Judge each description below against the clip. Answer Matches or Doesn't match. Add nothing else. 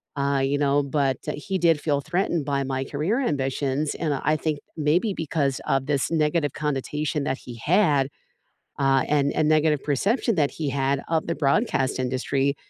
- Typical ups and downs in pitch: Doesn't match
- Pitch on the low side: Doesn't match